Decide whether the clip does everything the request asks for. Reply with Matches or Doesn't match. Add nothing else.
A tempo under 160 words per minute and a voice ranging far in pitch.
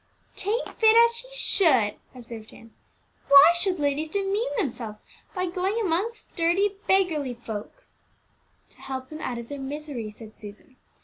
Matches